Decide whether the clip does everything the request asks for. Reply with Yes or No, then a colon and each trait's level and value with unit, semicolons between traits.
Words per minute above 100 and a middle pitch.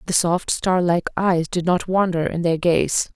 Yes: fast, 205 wpm; medium, 175 Hz